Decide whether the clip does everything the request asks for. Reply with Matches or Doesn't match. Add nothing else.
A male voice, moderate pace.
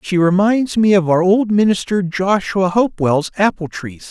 Matches